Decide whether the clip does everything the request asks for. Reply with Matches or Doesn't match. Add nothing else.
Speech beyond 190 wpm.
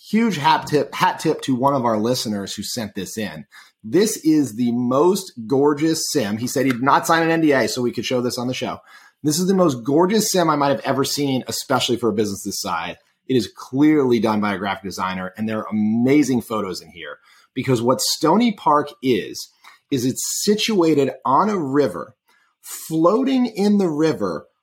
Matches